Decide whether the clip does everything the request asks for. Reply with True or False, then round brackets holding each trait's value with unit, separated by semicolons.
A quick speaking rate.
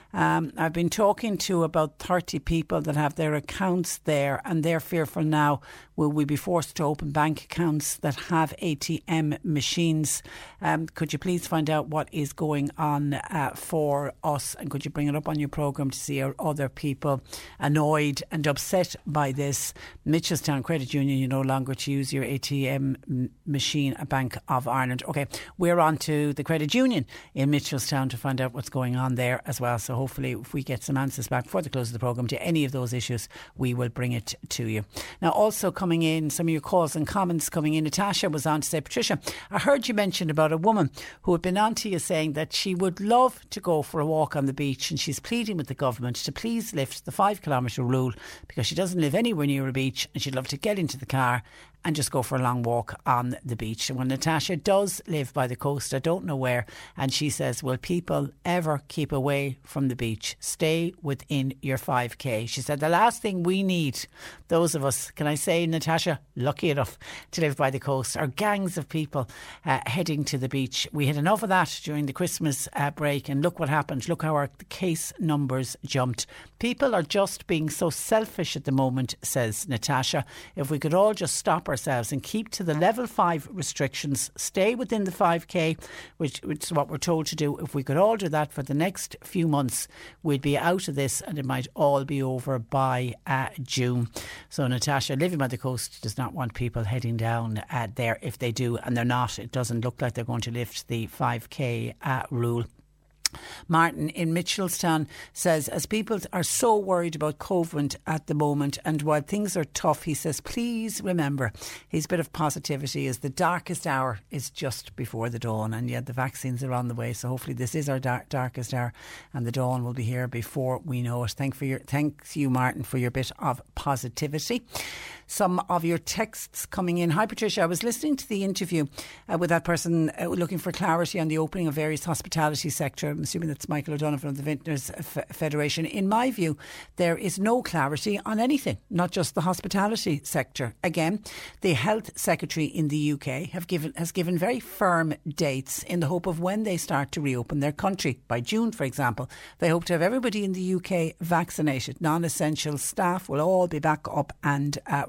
True (210 wpm)